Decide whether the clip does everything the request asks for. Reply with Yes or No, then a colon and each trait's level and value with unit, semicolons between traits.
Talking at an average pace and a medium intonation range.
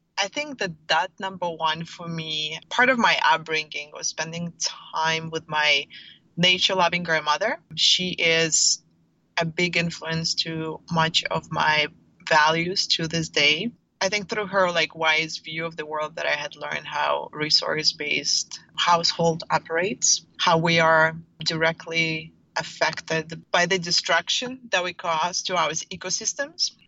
No: average, 145 wpm; narrow, 2.2 semitones